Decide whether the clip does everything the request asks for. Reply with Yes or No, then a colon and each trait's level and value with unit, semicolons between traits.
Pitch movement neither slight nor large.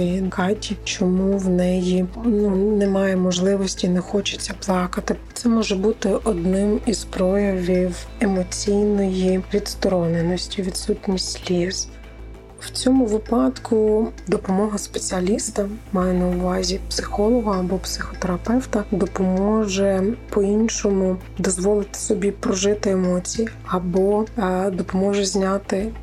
No: narrow, 2.2 semitones